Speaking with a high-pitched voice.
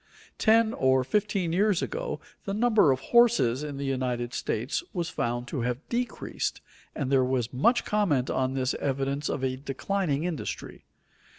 No: medium, 140 Hz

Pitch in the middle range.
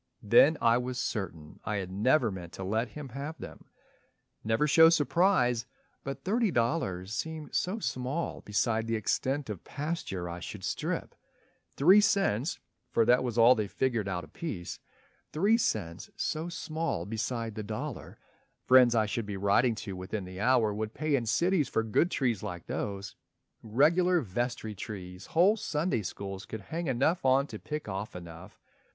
No: low, 115 Hz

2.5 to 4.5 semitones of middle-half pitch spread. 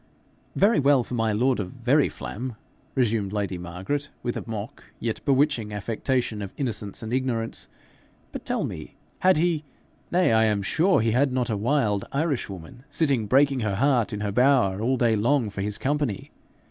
No: average, 4.9 semitones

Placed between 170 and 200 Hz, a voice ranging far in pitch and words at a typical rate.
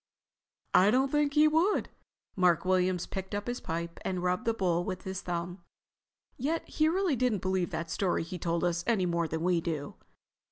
Yes: medium, 185 Hz; wide, 5.7 semitones; average, 190 wpm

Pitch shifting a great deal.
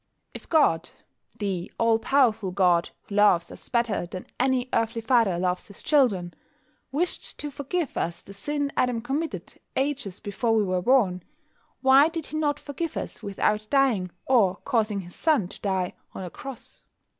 Yes: wide, 6.3 semitones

